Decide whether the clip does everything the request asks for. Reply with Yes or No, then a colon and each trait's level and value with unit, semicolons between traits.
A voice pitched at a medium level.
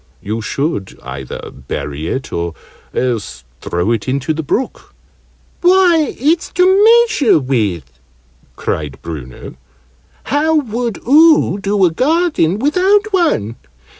Yes: medium, 170 Hz